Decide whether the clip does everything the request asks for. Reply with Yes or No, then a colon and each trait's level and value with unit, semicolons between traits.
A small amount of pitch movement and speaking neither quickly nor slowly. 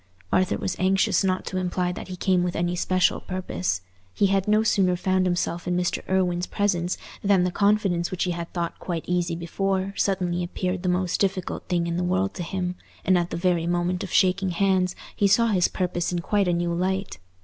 No: narrow, 1.5 semitones; fast, 210 wpm